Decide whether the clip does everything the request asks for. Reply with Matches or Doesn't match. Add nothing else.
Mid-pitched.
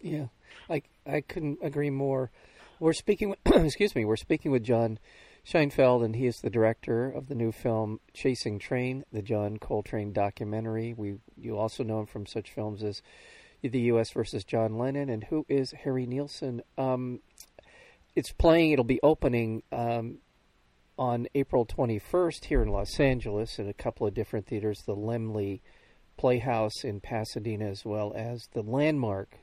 Doesn't match